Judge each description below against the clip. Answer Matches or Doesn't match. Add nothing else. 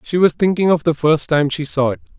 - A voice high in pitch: Doesn't match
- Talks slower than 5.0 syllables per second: Doesn't match